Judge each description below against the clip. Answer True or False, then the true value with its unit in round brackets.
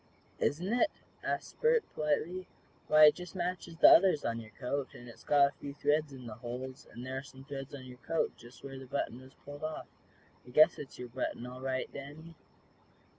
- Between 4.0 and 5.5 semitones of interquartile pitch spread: False (3.5 semitones)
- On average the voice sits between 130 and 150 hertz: True (140 Hz)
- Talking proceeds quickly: True (210 wpm)